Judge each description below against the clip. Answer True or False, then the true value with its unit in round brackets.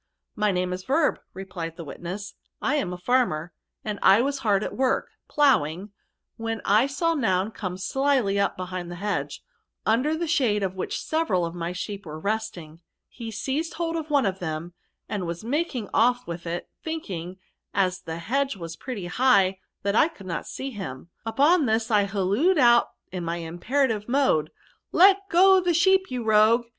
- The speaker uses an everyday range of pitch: False (6.9 semitones)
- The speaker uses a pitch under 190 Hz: False (210 Hz)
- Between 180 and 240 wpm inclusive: True (190 wpm)